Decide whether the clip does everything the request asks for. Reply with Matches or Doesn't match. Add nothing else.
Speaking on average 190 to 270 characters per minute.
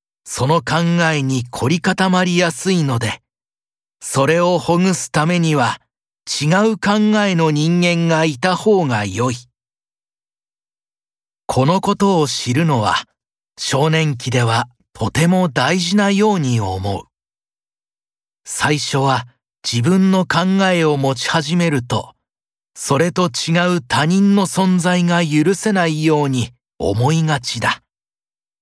Matches